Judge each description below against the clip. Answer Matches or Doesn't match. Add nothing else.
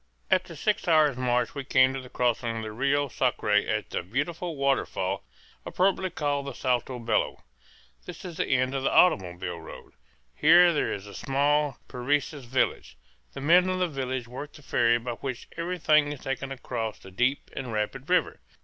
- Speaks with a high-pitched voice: Doesn't match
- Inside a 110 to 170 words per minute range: Doesn't match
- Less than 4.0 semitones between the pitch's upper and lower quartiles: Matches